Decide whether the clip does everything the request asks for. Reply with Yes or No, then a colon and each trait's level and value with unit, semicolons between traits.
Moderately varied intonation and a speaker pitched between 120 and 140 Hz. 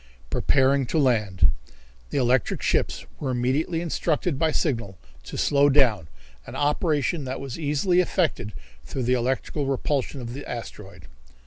Yes: average, 3.7 semitones; low, 135 Hz